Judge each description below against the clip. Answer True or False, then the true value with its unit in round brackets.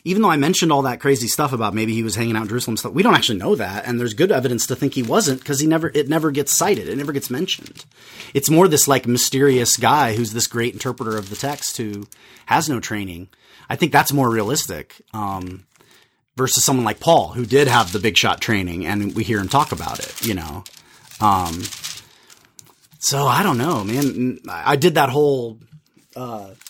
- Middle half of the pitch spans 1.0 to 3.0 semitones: False (4.3 semitones)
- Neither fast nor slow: False (215 wpm)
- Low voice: True (125 Hz)